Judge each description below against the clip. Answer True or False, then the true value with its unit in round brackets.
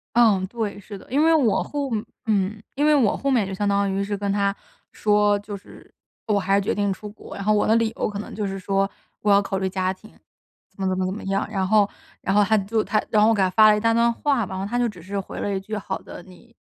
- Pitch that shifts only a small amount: True (2.0 semitones)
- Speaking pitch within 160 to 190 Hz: False (205 Hz)